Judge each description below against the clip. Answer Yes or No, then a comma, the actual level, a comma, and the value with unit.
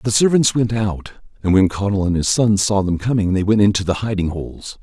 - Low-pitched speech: Yes, low, 100 Hz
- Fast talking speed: Yes, fast, 235 wpm